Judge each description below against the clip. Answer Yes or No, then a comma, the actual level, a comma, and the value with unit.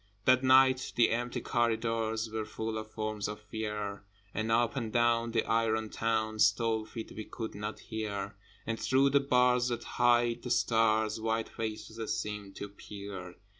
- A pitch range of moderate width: No, narrow, 1.6 semitones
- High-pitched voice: No, low, 110 Hz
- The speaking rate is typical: Yes, average, 165 wpm